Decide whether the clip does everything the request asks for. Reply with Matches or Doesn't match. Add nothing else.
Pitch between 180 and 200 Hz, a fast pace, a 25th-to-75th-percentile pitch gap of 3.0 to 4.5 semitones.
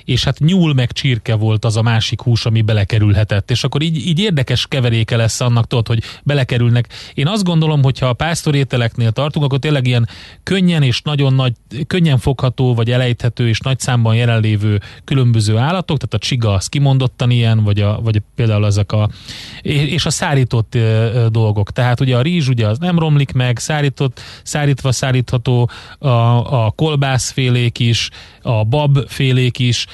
Doesn't match